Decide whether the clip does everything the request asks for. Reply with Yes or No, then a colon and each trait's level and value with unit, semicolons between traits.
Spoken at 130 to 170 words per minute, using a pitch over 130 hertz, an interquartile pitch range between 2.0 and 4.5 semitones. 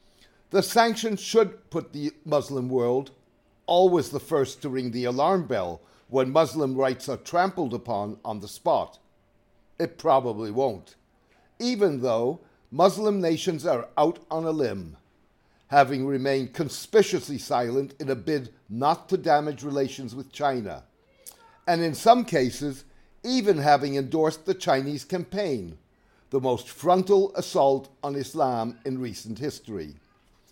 No: slow, 135 wpm; medium, 140 Hz; wide, 5.5 semitones